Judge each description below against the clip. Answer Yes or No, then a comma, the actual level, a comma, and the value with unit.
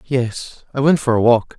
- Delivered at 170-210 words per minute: No, fast, 230 wpm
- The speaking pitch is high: No, low, 125 Hz